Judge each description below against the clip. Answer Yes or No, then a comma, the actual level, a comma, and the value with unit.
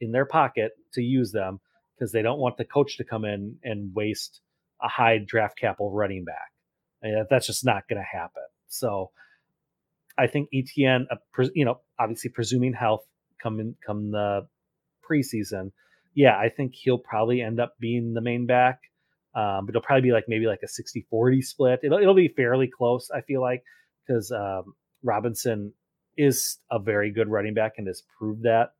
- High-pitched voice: No, low, 120 Hz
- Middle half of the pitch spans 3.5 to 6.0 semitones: No, average, 2.9 semitones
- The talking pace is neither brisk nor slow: Yes, average, 190 wpm